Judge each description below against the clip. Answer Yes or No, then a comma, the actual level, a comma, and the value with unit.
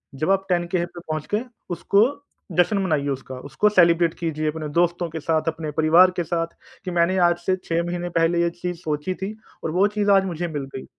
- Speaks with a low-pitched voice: No, medium, 170 Hz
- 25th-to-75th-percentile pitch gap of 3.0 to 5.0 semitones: No, narrow, 2.4 semitones